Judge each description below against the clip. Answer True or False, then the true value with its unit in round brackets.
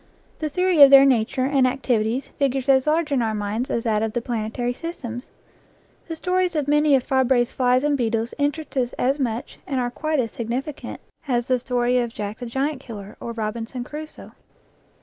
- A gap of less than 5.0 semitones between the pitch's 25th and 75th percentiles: True (3.4 semitones)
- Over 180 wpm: True (195 wpm)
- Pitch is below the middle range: False (255 Hz)